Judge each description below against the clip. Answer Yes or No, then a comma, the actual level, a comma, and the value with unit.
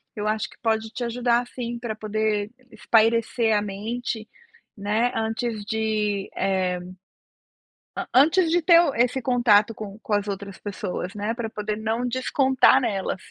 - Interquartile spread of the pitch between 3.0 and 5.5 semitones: No, narrow, 2.6 semitones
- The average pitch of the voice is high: Yes, high, 220 Hz